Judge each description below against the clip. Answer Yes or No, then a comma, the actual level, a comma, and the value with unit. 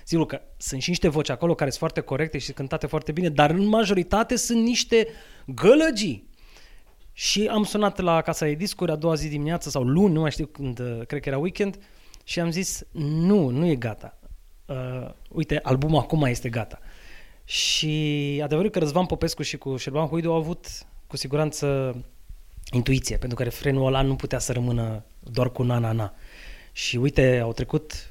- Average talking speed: No, fast, 175 wpm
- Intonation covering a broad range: No, average, 4.7 semitones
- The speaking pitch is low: No, medium, 150 Hz